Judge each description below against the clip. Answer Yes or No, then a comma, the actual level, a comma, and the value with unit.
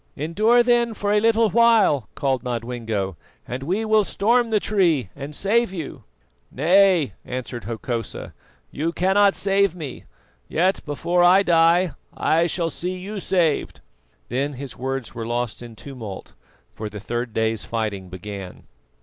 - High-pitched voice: No, medium, 155 Hz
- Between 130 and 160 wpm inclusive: Yes, average, 140 wpm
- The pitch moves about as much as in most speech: No, wide, 8.5 semitones